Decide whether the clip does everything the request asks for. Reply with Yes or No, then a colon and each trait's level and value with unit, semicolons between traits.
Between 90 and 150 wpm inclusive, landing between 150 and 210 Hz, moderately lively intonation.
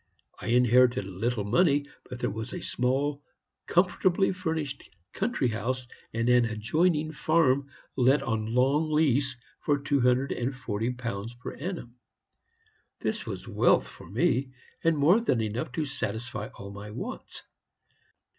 No: average, 145 wpm; low, 130 Hz; average, 4.1 semitones